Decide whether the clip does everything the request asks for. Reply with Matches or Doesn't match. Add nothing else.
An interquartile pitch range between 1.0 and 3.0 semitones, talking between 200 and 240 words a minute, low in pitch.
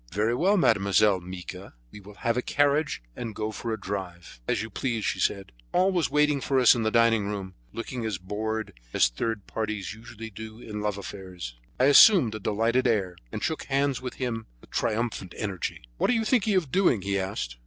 Doesn't match